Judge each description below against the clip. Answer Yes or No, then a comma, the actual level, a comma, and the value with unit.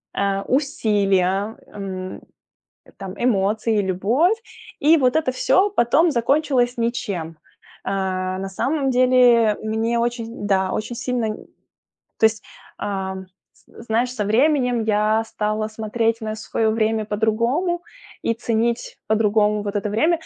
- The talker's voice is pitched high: Yes, high, 220 Hz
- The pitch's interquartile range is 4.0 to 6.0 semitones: No, average, 3.2 semitones